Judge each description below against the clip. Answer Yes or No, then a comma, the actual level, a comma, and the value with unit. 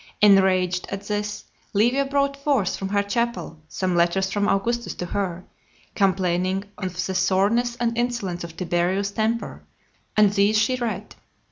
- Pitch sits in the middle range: No, high, 200 Hz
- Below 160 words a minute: Yes, average, 145 wpm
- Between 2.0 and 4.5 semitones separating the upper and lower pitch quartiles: Yes, average, 3.9 semitones